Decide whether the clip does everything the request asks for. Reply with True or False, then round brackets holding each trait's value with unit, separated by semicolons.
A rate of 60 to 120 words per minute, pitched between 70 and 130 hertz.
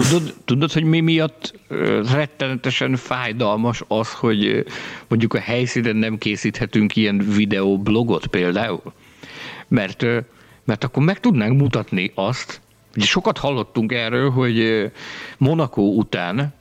True (110 wpm; 120 Hz)